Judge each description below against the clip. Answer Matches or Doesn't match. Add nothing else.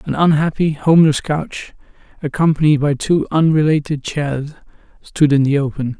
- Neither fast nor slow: Doesn't match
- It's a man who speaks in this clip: Matches